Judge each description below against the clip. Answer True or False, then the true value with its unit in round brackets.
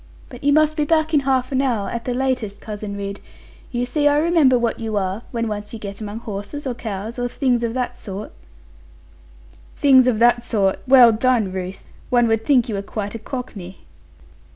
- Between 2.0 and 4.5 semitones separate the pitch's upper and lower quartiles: True (3.9 semitones)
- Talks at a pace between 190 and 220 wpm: True (200 wpm)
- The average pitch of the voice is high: True (235 Hz)